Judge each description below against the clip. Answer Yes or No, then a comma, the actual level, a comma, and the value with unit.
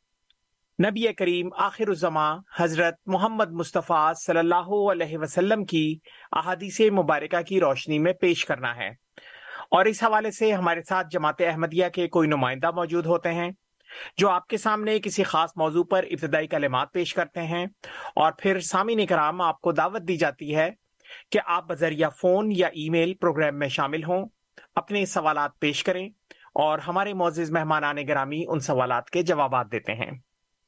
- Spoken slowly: No, average, 165 wpm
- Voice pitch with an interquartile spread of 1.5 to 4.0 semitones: Yes, average, 3.3 semitones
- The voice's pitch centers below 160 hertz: No, medium, 175 Hz